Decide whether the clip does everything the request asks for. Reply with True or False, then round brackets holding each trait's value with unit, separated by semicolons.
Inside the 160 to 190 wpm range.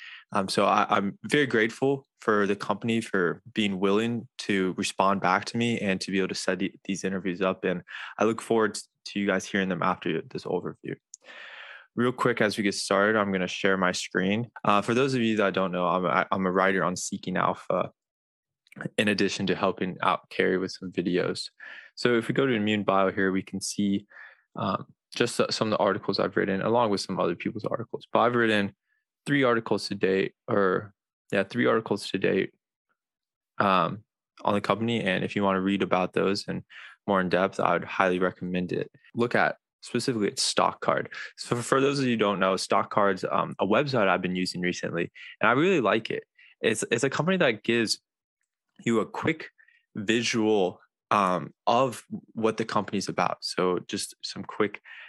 False (200 wpm)